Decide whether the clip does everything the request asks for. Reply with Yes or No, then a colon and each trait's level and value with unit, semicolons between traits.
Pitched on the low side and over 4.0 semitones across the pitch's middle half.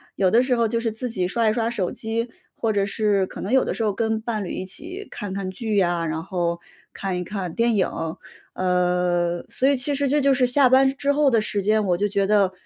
No: high, 215 Hz; average, 4.5 semitones